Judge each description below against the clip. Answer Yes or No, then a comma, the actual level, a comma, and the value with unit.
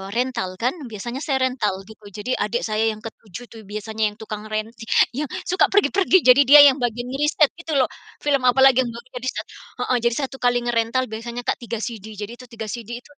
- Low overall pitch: No, high, 240 Hz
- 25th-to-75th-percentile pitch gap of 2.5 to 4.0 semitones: Yes, average, 3.3 semitones